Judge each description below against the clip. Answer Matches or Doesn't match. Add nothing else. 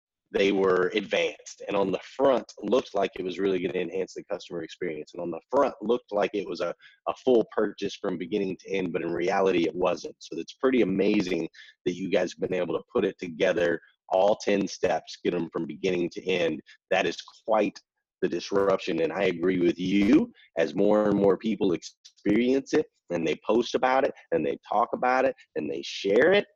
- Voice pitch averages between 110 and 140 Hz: Doesn't match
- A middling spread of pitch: Doesn't match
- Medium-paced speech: Doesn't match